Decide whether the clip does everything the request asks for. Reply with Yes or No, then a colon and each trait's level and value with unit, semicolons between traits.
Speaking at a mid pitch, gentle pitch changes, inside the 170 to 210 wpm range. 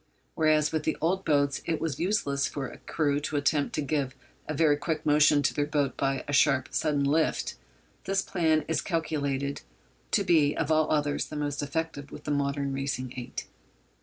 Yes: medium, 145 Hz; narrow, 1.9 semitones; average, 190 wpm